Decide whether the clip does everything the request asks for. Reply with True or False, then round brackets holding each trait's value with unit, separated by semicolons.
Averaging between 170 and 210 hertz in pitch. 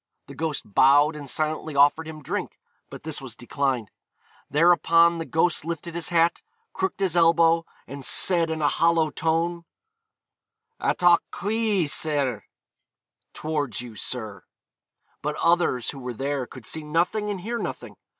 False (160 Hz)